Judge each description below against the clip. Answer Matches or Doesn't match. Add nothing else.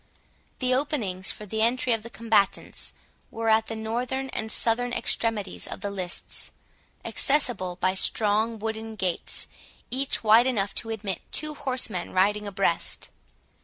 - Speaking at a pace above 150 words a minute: Doesn't match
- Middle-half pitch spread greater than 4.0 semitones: Doesn't match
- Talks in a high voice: Matches